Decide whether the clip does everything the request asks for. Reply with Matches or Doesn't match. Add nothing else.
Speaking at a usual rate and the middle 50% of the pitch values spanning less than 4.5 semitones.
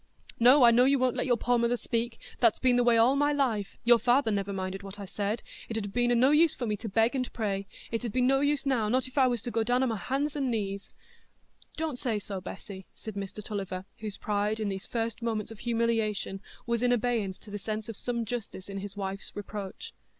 Doesn't match